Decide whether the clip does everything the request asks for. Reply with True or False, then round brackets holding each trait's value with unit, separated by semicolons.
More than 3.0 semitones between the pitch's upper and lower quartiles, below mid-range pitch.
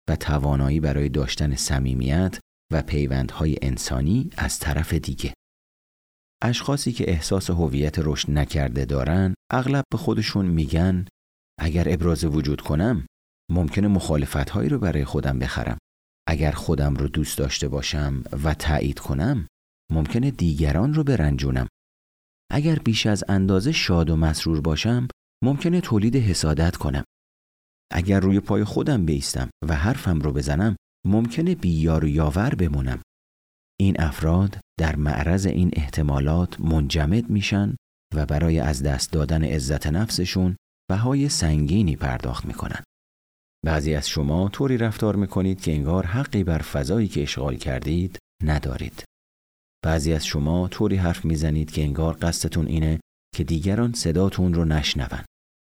True (4.8 semitones; 80 Hz)